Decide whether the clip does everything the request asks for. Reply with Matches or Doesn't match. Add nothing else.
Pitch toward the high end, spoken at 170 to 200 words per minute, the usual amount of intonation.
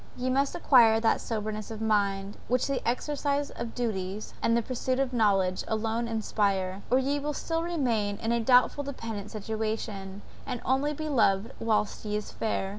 Matches